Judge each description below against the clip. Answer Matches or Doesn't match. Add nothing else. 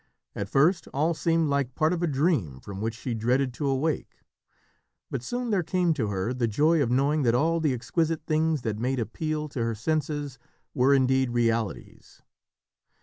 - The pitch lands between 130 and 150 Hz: Matches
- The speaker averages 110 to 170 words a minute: Doesn't match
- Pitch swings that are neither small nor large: Matches